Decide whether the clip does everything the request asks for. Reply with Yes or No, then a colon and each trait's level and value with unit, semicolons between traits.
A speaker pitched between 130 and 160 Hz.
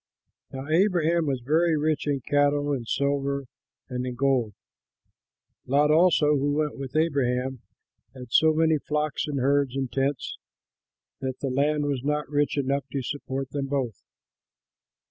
Yes: medium, 140 Hz